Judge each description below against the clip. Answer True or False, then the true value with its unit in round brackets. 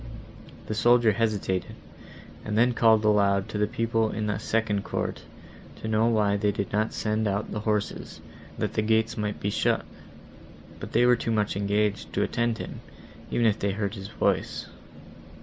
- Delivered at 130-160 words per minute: False (185 wpm)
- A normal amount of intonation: False (1.7 semitones)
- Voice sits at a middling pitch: False (110 Hz)